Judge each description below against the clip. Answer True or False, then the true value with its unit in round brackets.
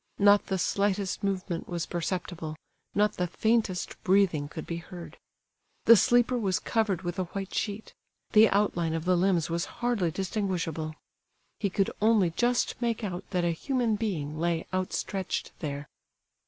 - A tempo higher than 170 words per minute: False (155 wpm)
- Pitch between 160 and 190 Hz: True (185 Hz)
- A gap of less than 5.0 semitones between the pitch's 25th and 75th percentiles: True (3.6 semitones)